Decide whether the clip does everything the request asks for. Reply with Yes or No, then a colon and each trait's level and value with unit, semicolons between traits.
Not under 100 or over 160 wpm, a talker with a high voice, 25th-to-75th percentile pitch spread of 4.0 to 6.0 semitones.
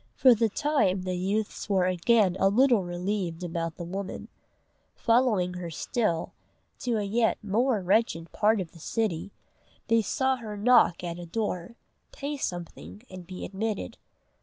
Yes: average, 155 wpm; high, 200 Hz; average, 4.3 semitones